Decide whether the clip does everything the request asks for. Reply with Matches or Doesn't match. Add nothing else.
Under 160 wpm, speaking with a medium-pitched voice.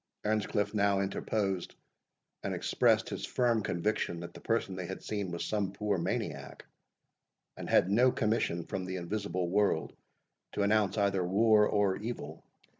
Doesn't match